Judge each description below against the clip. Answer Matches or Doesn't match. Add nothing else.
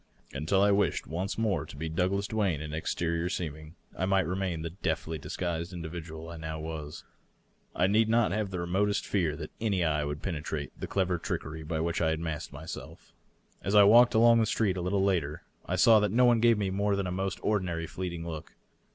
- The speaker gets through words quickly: Matches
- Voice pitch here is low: Matches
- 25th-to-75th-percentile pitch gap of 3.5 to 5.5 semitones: Matches